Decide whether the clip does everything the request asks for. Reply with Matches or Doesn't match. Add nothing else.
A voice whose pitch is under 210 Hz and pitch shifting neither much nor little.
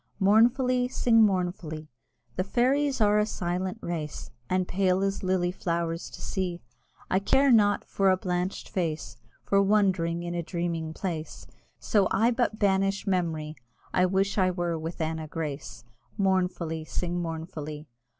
Matches